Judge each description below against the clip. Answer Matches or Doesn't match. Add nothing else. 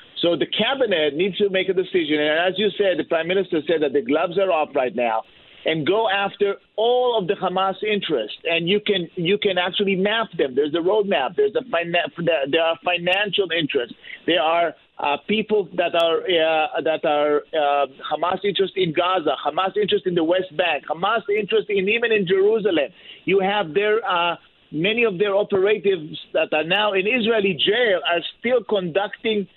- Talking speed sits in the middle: Matches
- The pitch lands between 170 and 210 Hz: Matches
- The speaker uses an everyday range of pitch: Matches